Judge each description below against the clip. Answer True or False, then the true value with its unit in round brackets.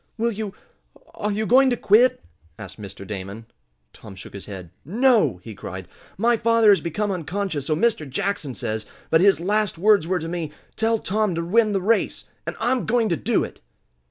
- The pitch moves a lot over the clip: True (7.5 semitones)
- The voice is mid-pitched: False (195 Hz)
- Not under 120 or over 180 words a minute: False (190 wpm)